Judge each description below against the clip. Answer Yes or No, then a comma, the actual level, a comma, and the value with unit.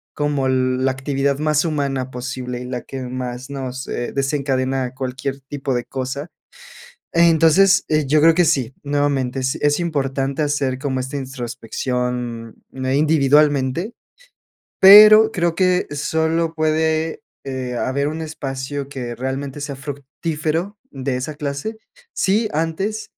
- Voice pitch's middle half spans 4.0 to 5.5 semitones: No, average, 3.2 semitones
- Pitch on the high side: No, medium, 140 Hz